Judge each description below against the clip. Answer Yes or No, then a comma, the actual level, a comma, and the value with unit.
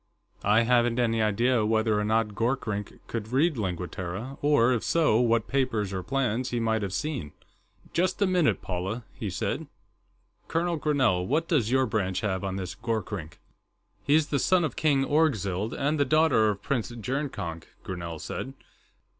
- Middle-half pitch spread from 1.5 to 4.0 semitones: No, average, 5.2 semitones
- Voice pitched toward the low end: Yes, low, 115 Hz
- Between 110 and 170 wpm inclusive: Yes, average, 165 wpm